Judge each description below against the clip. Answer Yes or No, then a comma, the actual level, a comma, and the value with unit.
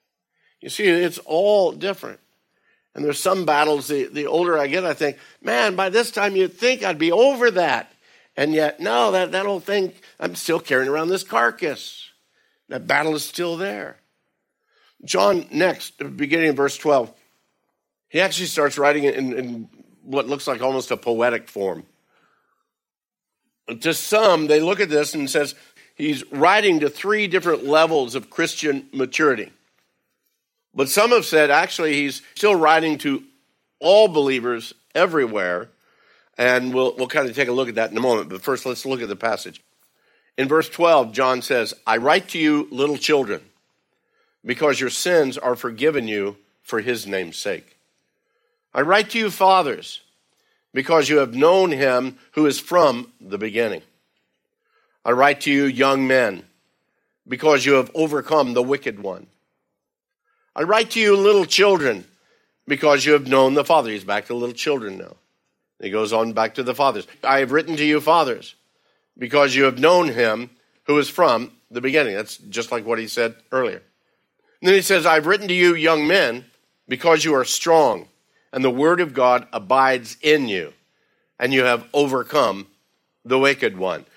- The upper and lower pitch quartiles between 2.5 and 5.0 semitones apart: No, wide, 5.4 semitones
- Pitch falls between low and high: Yes, medium, 145 Hz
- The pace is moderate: Yes, average, 170 wpm